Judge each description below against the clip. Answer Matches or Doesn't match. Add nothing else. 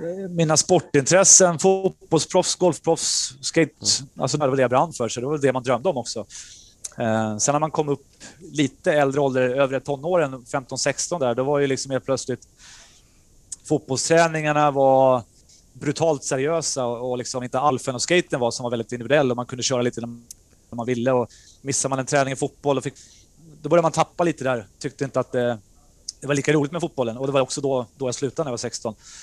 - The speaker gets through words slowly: Doesn't match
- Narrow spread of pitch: Doesn't match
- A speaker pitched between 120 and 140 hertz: Matches